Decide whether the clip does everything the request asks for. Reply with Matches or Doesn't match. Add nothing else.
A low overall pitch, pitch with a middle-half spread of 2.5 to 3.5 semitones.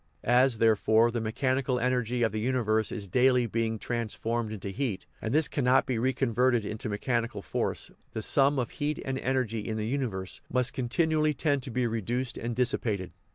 Matches